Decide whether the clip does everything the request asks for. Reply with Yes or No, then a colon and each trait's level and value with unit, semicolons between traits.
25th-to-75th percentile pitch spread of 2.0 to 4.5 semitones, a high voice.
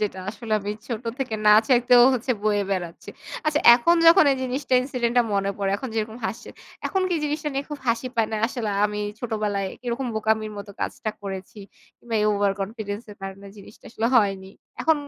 Yes: average, 3.7 semitones; high, 220 Hz